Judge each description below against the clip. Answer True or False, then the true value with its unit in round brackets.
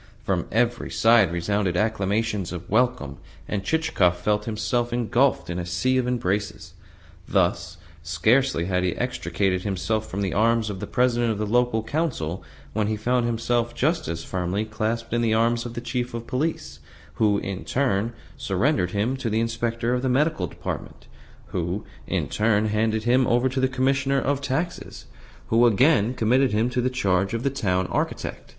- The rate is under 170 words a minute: False (175 wpm)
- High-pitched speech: False (115 Hz)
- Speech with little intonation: False (3.9 semitones)